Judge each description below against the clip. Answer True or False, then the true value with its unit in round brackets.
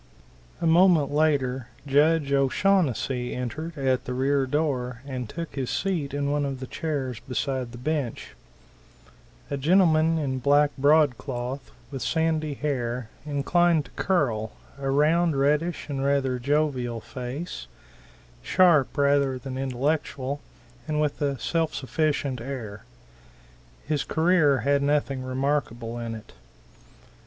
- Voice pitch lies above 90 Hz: True (140 Hz)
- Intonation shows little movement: False (3.1 semitones)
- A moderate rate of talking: False (125 wpm)